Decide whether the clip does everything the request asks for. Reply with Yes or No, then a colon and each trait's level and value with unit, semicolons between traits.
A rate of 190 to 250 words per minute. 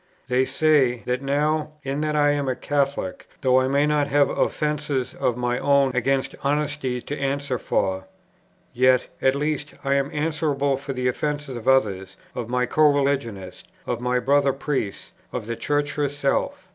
No: average, 170 wpm